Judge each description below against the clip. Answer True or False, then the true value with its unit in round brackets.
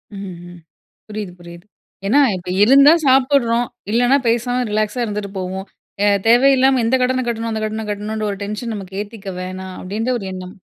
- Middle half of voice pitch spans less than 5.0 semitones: True (3.9 semitones)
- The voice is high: True (215 Hz)